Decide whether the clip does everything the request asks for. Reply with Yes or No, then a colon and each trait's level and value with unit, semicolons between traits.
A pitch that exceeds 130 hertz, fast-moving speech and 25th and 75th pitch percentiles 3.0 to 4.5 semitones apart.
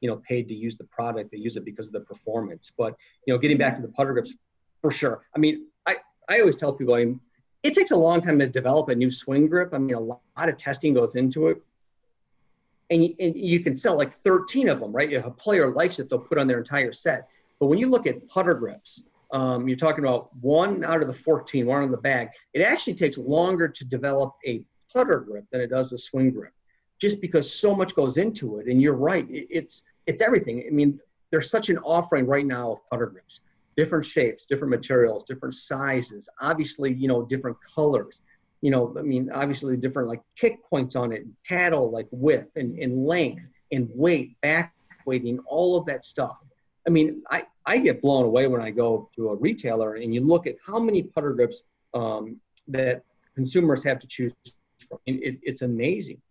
No: medium, 140 Hz; fast, 220 wpm; average, 5.0 semitones